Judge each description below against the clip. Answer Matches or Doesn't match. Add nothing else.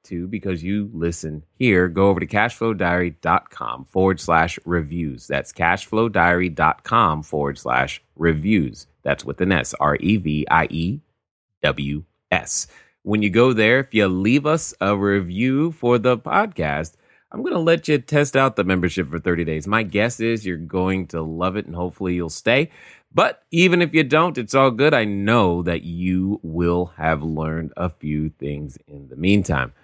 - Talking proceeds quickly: Doesn't match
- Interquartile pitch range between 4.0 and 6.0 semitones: Matches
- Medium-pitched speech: Doesn't match